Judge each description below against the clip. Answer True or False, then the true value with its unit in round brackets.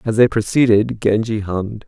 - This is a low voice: True (110 Hz)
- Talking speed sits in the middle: True (160 wpm)